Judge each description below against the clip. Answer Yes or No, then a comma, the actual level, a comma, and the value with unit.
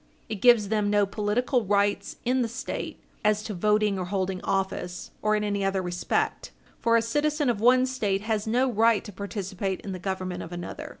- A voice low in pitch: No, high, 210 Hz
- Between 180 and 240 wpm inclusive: Yes, average, 195 wpm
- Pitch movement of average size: Yes, average, 3.1 semitones